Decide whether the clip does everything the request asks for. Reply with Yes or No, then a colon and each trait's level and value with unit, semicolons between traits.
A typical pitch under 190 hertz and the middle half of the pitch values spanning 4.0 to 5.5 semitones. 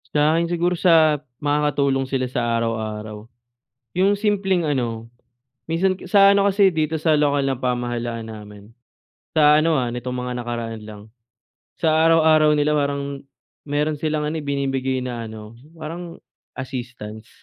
Yes: medium, 140 Hz; average, 4.9 semitones